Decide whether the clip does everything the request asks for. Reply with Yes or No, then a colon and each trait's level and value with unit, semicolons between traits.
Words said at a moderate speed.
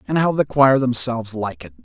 No: fast, 230 wpm